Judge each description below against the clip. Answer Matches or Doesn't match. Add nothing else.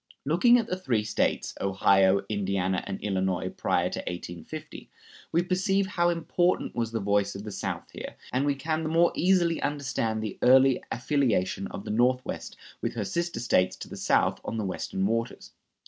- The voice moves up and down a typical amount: Doesn't match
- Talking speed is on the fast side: Doesn't match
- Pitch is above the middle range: Doesn't match